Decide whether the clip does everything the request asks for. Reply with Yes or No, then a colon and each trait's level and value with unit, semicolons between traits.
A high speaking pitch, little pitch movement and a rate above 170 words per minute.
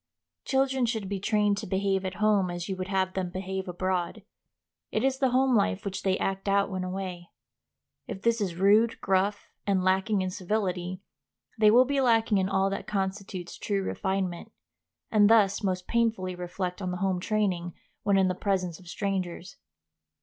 Yes: high, 195 Hz; narrow, 2.3 semitones; average, 180 wpm